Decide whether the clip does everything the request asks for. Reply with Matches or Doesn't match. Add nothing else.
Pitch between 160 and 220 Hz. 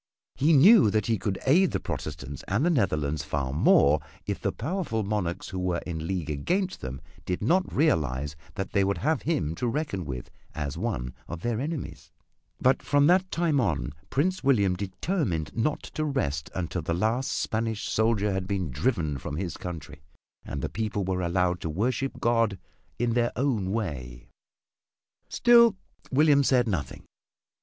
Doesn't match